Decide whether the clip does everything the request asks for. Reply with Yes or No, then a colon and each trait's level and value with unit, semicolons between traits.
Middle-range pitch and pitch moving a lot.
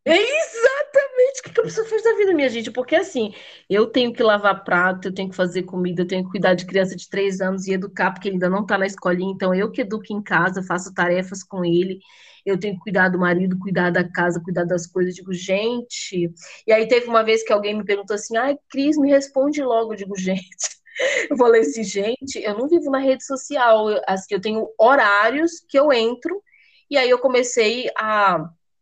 No: high, 210 Hz; wide, 5.7 semitones